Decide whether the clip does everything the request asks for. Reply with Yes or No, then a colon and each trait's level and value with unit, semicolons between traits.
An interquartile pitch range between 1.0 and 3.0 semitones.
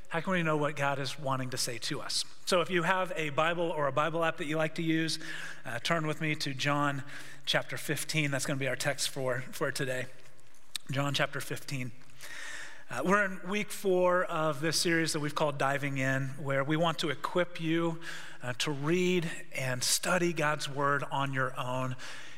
No: average, 3.4 semitones